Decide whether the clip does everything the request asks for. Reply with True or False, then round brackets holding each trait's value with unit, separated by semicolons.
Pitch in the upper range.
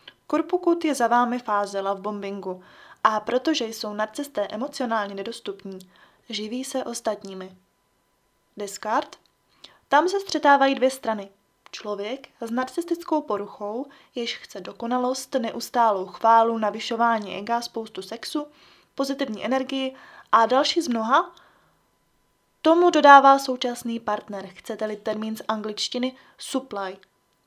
True (235 Hz)